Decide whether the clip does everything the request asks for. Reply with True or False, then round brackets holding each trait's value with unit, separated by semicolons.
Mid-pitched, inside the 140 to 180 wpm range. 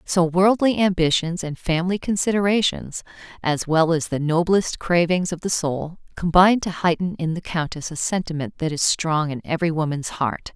True (170 Hz; 170 wpm)